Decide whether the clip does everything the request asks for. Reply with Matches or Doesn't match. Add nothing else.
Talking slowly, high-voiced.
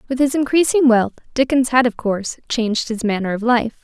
Doesn't match